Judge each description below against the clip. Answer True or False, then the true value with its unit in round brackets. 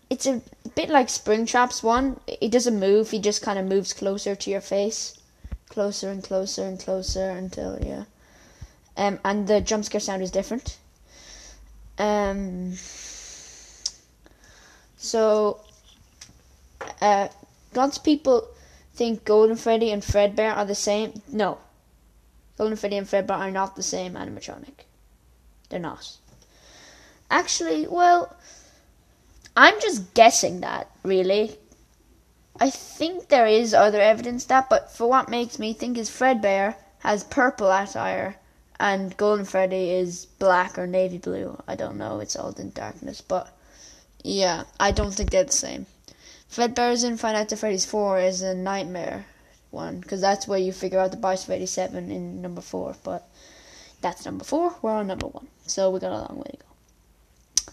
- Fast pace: False (150 wpm)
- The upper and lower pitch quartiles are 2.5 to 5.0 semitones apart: True (3.6 semitones)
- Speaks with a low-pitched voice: False (205 Hz)